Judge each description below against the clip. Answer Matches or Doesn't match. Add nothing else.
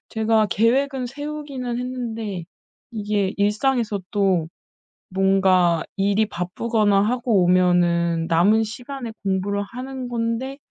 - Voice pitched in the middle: Doesn't match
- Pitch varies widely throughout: Doesn't match